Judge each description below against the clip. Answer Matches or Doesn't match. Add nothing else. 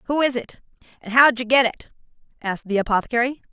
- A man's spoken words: Doesn't match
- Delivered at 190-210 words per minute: Matches